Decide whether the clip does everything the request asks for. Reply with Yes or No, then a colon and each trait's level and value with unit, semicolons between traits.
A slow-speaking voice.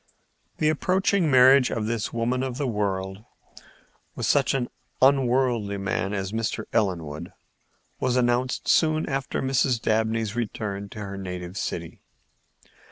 Yes: slow, 130 wpm